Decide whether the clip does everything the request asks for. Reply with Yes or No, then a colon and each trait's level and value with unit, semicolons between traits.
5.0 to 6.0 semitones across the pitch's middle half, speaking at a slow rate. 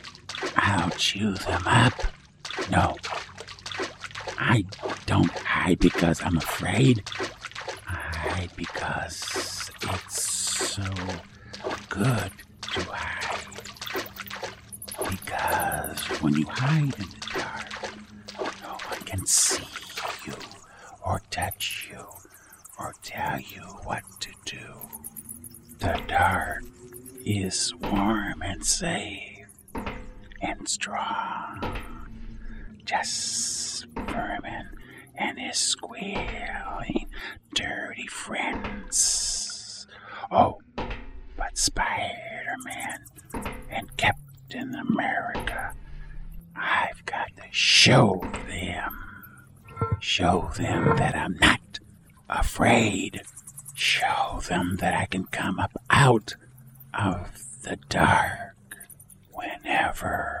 No: average, 4.5 semitones; slow, 80 wpm